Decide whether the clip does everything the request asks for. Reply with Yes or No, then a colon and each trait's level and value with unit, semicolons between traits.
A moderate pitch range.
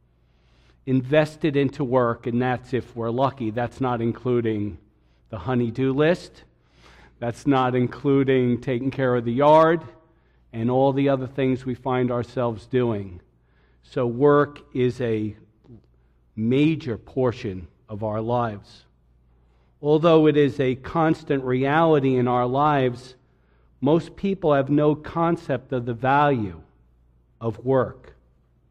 Yes: average, 4.3 semitones